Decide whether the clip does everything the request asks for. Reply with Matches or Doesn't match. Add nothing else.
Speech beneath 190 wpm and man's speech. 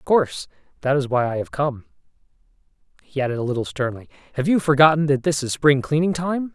Doesn't match